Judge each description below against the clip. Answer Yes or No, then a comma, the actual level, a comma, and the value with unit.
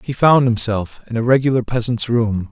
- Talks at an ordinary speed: Yes, average, 190 wpm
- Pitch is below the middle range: Yes, low, 120 Hz